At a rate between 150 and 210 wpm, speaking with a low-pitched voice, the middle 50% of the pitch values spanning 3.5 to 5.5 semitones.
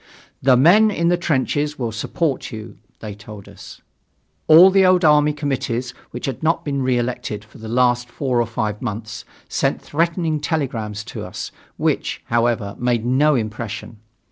Yes: average, 160 wpm; low, 125 Hz; average, 4.9 semitones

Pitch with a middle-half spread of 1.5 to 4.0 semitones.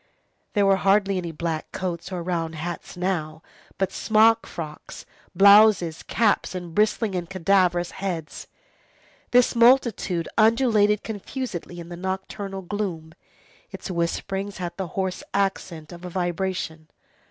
Yes: average, 3.0 semitones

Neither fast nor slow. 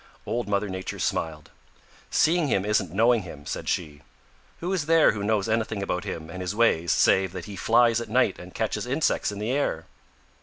Yes: average, 195 wpm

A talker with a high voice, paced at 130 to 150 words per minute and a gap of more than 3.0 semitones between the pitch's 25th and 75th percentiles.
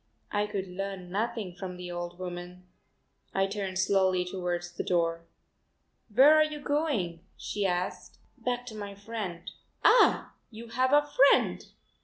Yes: high, 195 Hz; average, 145 wpm; average, 4.4 semitones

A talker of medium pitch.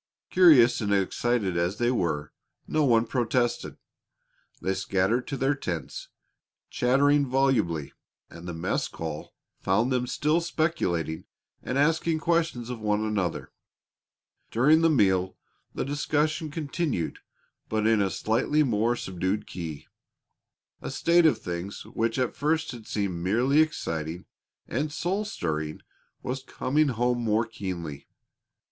No: low, 120 Hz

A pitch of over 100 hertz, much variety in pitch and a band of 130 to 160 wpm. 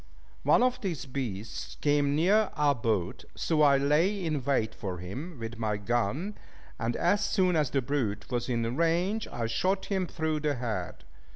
No: medium, 140 Hz; wide, 7.0 semitones; average, 175 wpm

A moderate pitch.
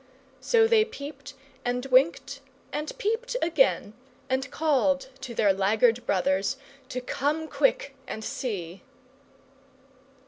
No: very high, 265 Hz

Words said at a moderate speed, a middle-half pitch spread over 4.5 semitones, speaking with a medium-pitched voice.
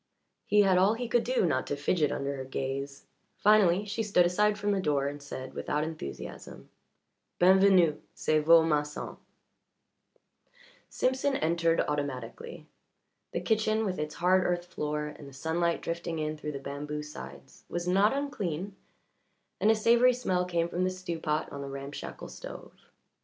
Yes: average, 165 wpm; average, 4.9 semitones; medium, 170 Hz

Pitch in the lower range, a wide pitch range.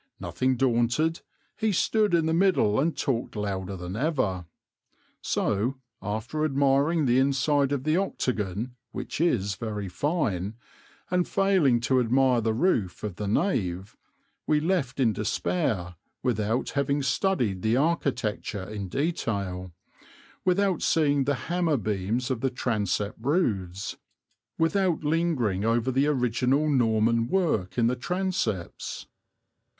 Yes: low, 125 Hz; wide, 6.6 semitones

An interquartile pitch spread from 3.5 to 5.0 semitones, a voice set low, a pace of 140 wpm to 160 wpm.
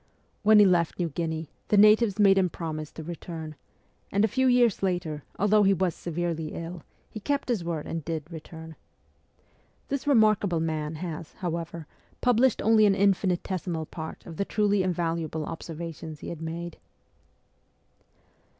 No: average, 3.9 semitones; medium, 175 Hz; average, 150 wpm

